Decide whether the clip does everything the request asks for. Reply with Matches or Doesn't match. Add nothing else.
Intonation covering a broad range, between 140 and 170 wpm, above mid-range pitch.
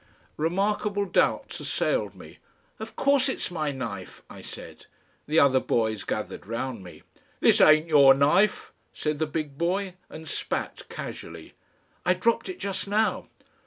Doesn't match